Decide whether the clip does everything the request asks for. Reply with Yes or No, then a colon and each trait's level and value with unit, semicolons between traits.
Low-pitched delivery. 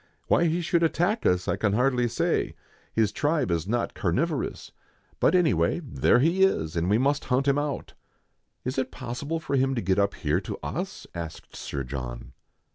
Yes: low, 125 Hz